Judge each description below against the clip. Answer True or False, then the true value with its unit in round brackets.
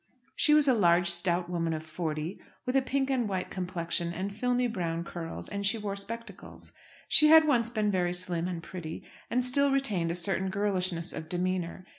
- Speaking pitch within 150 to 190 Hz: True (185 Hz)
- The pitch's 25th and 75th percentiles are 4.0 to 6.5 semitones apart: True (5.3 semitones)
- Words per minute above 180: True (190 wpm)